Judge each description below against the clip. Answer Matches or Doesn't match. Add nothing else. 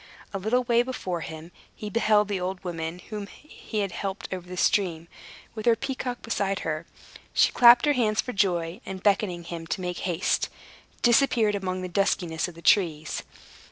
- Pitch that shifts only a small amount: Doesn't match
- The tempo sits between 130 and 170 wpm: Doesn't match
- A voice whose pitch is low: Doesn't match